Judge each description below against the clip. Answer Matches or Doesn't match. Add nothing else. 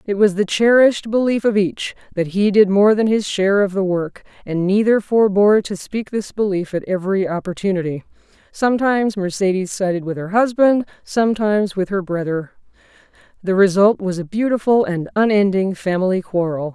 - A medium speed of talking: Matches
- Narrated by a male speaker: Doesn't match